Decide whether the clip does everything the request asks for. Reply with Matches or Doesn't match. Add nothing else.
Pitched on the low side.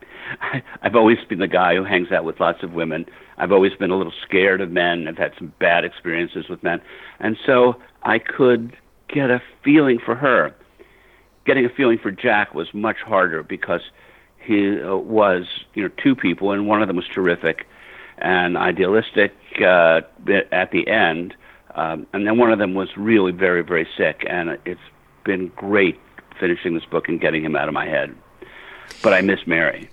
Matches